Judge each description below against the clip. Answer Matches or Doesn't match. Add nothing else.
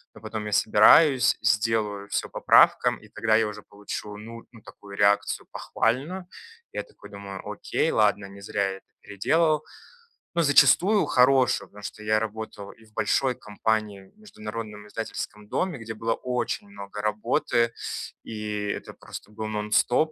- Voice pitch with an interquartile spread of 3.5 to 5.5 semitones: Doesn't match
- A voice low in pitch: Matches